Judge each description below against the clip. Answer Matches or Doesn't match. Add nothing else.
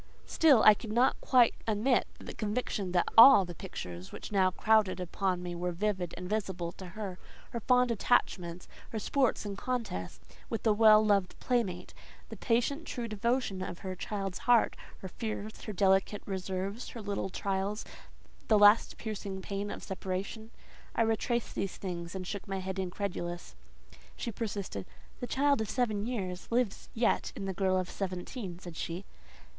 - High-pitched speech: Matches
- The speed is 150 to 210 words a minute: Matches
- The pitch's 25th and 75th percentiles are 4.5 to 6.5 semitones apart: Doesn't match